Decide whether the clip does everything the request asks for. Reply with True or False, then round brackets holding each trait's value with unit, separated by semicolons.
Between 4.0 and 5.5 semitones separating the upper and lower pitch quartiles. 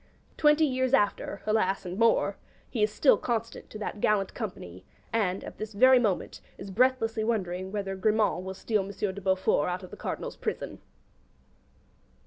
False (3.2 semitones)